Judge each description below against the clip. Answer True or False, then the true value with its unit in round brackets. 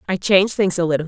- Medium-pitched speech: True (180 Hz)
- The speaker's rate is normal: False (280 wpm)